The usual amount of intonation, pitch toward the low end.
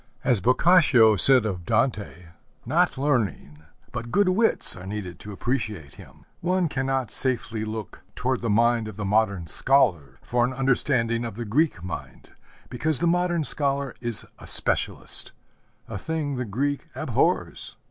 Yes: average, 4.8 semitones; low, 120 Hz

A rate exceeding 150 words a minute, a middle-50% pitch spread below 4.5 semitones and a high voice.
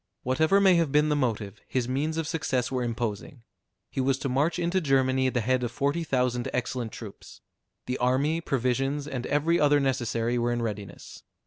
No: average, 190 wpm; average, 3.4 semitones; low, 130 Hz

